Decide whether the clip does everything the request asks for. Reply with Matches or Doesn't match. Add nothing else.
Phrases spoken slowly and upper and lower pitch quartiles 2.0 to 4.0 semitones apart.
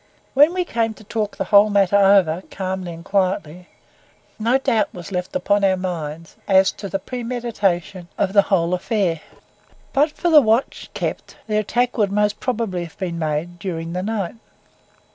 Doesn't match